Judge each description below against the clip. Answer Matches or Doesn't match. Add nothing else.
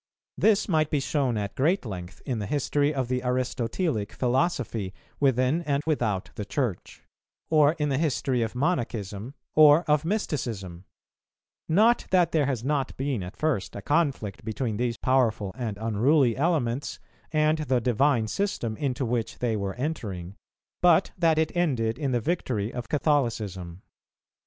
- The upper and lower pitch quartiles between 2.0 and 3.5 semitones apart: Doesn't match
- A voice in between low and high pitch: Doesn't match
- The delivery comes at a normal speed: Matches